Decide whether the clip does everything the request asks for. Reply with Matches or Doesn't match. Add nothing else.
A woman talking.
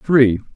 Doesn't match